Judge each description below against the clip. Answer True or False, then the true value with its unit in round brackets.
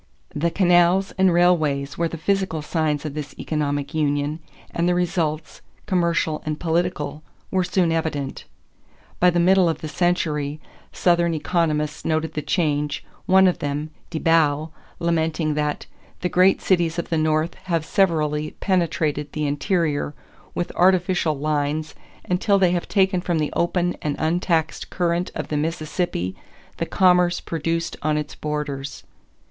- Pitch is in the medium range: True (165 Hz)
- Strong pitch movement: False (2.8 semitones)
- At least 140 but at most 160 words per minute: True (145 wpm)